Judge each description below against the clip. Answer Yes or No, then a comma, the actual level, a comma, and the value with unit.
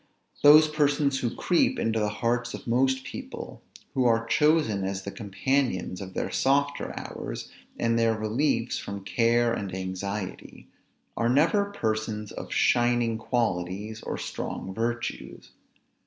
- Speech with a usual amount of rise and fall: Yes, average, 4.1 semitones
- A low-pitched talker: Yes, low, 115 Hz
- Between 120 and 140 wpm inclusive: Yes, slow, 135 wpm